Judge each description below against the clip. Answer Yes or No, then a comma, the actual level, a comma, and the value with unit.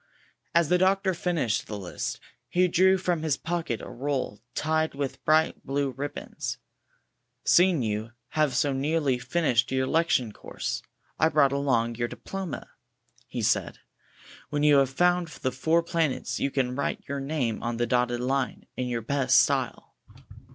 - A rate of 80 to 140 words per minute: No, average, 160 wpm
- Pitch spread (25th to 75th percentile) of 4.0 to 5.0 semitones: Yes, average, 4.7 semitones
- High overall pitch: No, medium, 140 Hz